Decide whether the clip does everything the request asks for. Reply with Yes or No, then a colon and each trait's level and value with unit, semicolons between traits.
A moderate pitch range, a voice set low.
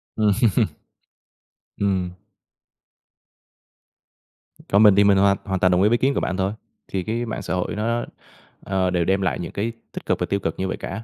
No: narrow, 2.3 semitones; low, 100 Hz